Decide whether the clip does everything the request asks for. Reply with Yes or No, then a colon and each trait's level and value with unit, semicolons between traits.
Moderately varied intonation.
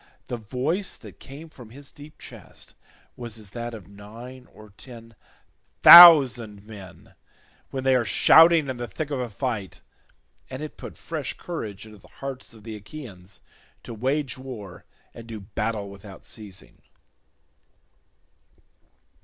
Yes: average, 4.5 semitones